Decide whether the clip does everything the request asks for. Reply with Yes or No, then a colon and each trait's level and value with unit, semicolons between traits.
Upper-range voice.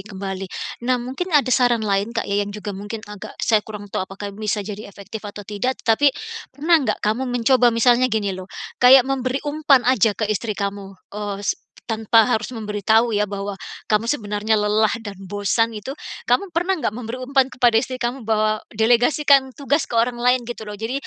Yes: high, 225 Hz